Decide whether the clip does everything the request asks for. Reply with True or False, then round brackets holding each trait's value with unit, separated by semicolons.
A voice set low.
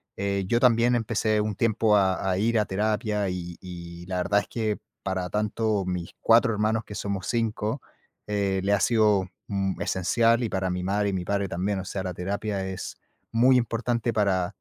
True (100 Hz)